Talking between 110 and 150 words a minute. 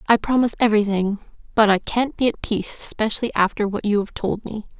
No: average, 200 wpm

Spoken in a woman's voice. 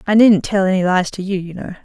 Yes: female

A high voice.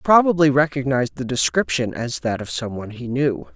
No: low, 130 Hz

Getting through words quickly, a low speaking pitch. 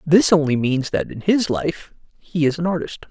No: fast, 215 wpm; medium, 160 Hz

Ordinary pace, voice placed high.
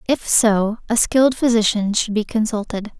Yes: average, 160 wpm; high, 220 Hz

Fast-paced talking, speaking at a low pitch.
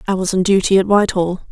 No: fast, 235 wpm; high, 190 Hz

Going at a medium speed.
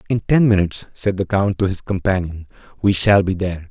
No: fast, 210 wpm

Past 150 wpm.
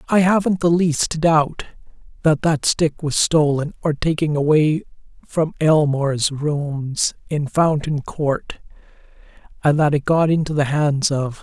No: average, 140 wpm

